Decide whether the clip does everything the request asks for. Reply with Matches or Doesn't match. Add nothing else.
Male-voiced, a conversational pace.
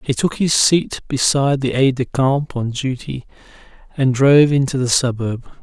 Matches